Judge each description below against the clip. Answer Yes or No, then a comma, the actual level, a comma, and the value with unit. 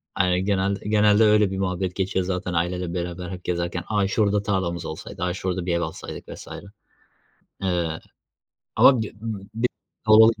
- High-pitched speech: No, very low, 95 Hz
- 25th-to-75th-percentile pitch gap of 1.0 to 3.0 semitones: Yes, average, 2.7 semitones